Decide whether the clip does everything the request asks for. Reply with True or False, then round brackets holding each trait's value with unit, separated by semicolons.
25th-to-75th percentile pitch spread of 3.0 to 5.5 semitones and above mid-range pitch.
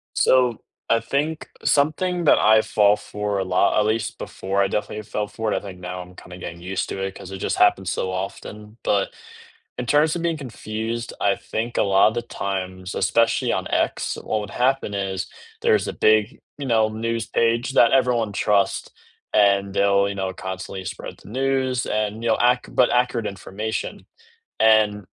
False (3.3 semitones; 105 Hz)